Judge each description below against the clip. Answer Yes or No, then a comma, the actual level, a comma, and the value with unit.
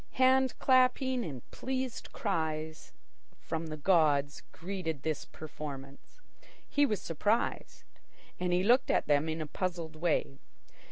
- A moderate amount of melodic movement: No, wide, 7.5 semitones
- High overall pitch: No, medium, 165 Hz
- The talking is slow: Yes, slow, 120 wpm